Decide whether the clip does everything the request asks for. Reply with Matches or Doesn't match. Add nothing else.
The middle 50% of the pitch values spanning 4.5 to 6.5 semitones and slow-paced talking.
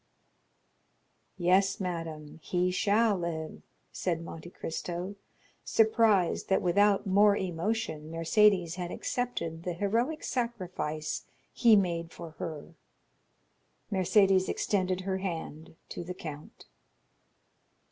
Doesn't match